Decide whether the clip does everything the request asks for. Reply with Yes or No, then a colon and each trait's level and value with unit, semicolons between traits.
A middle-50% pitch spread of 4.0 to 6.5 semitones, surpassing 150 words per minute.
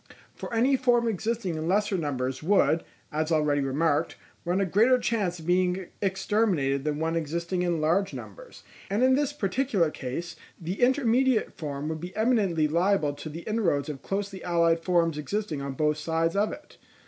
Yes: average, 5.3 semitones; average, 170 wpm